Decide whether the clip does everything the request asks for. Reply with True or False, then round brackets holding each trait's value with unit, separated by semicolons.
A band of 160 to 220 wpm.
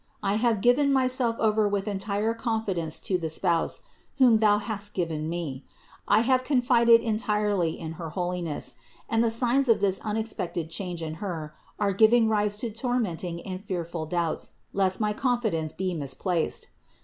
True (165 wpm)